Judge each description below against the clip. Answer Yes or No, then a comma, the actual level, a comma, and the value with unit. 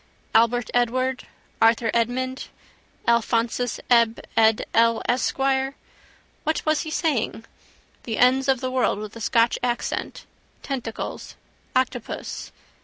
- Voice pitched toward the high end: Yes, high, 245 Hz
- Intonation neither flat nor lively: No, narrow, 2.2 semitones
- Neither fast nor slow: No, slow, 110 wpm